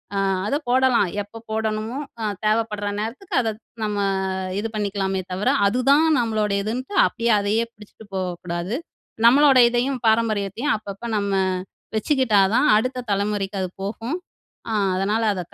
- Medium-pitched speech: No, high, 215 Hz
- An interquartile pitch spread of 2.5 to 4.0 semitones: Yes, average, 3.1 semitones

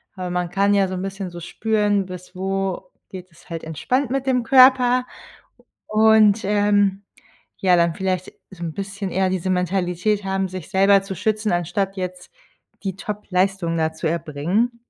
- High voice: Yes, high, 195 Hz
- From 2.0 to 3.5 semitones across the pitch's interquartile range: Yes, narrow, 2.6 semitones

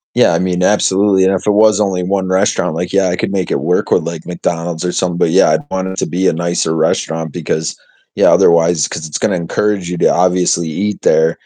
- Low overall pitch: Yes, very low, 90 Hz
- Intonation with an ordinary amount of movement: No, narrow, 2.2 semitones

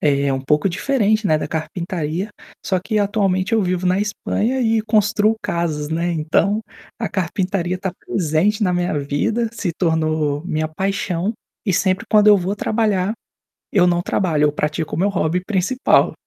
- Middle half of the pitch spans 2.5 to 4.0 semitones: No, average, 4.4 semitones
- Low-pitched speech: No, medium, 185 Hz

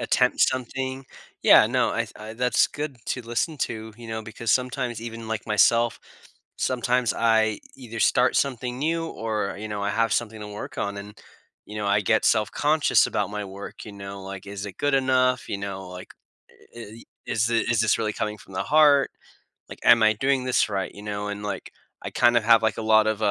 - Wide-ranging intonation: No, average, 3.3 semitones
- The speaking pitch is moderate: No, low, 110 Hz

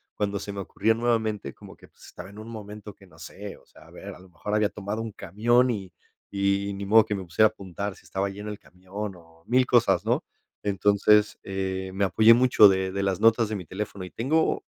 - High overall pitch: No, low, 100 Hz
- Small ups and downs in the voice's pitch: Yes, narrow, 2.1 semitones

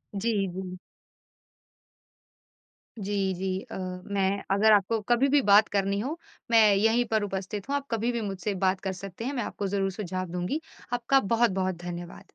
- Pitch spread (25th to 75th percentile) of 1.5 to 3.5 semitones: Yes, average, 3.2 semitones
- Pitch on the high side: Yes, high, 200 Hz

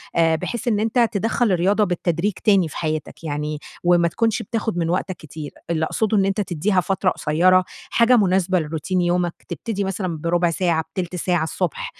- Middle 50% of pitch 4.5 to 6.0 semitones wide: No, average, 3.6 semitones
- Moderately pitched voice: Yes, medium, 180 Hz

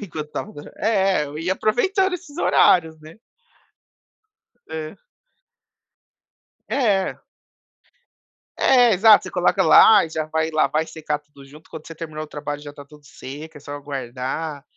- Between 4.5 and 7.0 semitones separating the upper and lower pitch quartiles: Yes, average, 4.8 semitones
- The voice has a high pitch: No, medium, 155 Hz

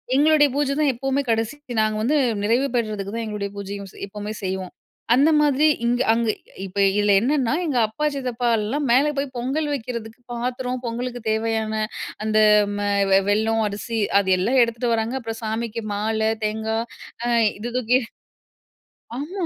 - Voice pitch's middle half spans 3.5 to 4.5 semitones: No, average, 3.1 semitones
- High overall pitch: Yes, high, 230 Hz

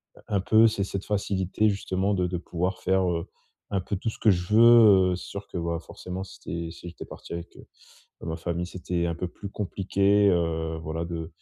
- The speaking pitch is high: No, very low, 90 Hz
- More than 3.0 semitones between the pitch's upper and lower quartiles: No, average, 2.7 semitones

